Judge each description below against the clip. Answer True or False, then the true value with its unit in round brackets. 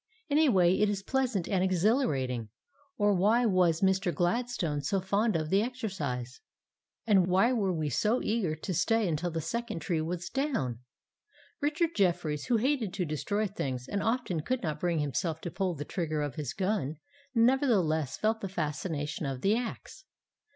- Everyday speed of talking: True (170 wpm)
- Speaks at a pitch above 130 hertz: True (185 Hz)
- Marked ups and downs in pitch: True (6.0 semitones)